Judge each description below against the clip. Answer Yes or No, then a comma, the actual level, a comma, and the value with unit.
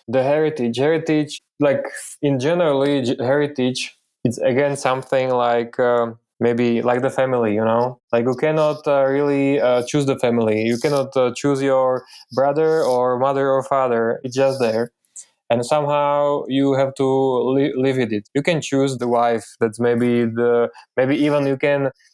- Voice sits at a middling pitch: No, low, 130 Hz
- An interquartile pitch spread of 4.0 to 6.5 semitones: No, average, 2.7 semitones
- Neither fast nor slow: No, fast, 170 wpm